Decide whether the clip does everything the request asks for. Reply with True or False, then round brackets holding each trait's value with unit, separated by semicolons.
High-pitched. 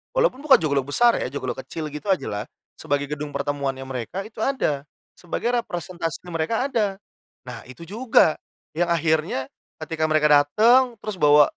False (160 Hz)